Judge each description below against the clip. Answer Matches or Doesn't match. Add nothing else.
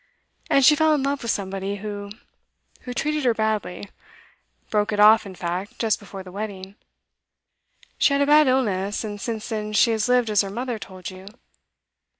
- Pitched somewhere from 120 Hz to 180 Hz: Doesn't match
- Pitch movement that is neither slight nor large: Matches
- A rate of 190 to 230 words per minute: Doesn't match